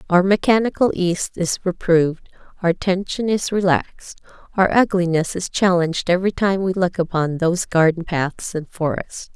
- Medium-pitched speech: Yes, medium, 180 Hz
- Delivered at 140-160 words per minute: Yes, average, 150 wpm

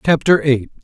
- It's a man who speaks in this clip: Yes, male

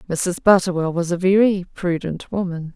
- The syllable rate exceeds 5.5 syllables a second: No, 4.8 syllables/s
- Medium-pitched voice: Yes, medium, 180 Hz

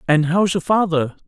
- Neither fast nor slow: Yes, average, 190 wpm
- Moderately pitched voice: Yes, medium, 170 Hz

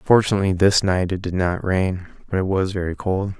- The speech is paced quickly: Yes, fast, 210 wpm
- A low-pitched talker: Yes, very low, 95 Hz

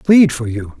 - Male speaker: Yes, male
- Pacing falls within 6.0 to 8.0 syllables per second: No, 4.4 syllables/s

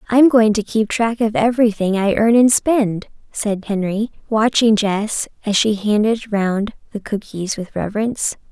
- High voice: Yes, high, 215 Hz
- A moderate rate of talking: Yes, average, 160 wpm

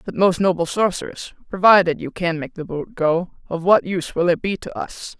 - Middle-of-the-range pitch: Yes, medium, 175 Hz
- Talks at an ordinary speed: No, fast, 220 wpm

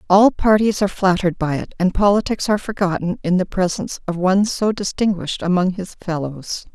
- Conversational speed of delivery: Yes, average, 180 wpm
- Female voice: Yes, female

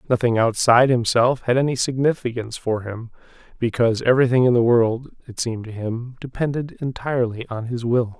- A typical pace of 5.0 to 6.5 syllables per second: Yes, 5.8 syllables/s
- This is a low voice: Yes, low, 120 Hz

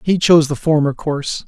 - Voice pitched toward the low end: No, medium, 155 Hz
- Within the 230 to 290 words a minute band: No, fast, 205 wpm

